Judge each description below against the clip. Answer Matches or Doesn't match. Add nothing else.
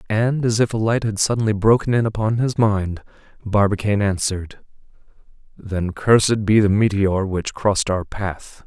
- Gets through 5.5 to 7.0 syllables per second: Doesn't match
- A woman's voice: Doesn't match